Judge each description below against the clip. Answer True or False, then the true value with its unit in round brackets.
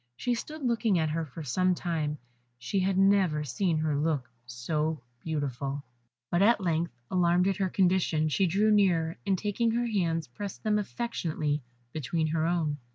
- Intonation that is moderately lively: True (4.2 semitones)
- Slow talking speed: False (165 wpm)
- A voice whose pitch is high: False (170 Hz)